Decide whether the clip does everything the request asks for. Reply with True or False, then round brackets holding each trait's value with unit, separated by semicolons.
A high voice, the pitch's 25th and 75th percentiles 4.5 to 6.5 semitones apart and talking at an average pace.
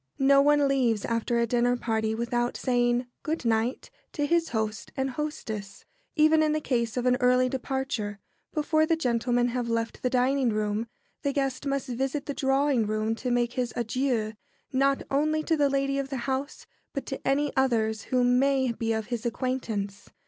False (250 Hz; 3.0 semitones; 180 wpm)